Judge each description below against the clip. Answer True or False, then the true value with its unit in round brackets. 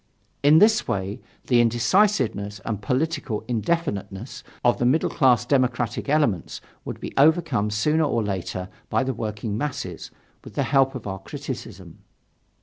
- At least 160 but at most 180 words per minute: False (145 wpm)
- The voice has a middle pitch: False (120 Hz)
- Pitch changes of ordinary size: False (5.9 semitones)